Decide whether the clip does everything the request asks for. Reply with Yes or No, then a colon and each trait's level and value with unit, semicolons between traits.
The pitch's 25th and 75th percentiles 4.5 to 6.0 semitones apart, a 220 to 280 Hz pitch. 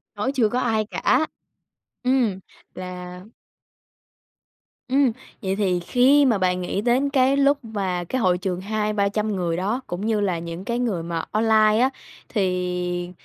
No: average, 5.1 semitones; high, 205 Hz